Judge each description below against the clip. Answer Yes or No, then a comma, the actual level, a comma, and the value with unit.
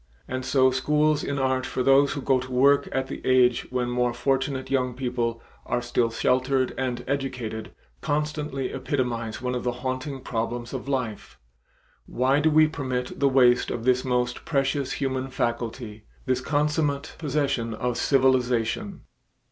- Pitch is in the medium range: No, low, 130 Hz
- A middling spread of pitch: No, narrow, 2.0 semitones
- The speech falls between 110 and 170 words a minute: Yes, average, 155 wpm